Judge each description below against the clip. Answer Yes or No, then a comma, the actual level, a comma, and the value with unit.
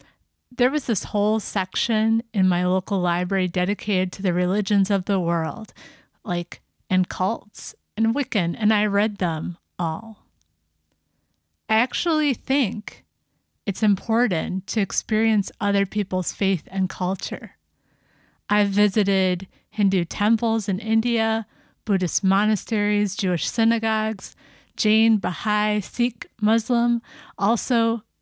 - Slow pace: Yes, slow, 115 wpm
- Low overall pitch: No, high, 205 Hz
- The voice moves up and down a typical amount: Yes, average, 3.2 semitones